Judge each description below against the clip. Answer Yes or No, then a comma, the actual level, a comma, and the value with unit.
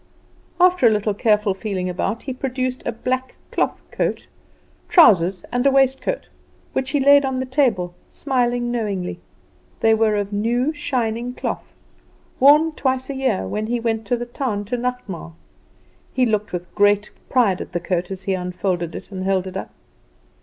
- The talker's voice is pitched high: Yes, high, 230 Hz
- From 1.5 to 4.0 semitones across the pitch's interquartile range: No, average, 4.9 semitones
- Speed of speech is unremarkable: Yes, average, 165 wpm